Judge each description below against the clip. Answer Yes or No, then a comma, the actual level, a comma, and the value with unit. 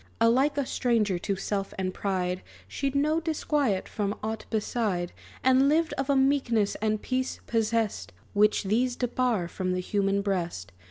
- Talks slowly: No, average, 155 wpm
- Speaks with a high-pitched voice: Yes, high, 220 Hz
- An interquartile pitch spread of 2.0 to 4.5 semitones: No, average, 5.0 semitones